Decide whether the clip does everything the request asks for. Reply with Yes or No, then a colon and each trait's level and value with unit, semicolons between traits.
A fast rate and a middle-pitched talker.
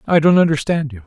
Yes: fast, 225 wpm; medium, 150 Hz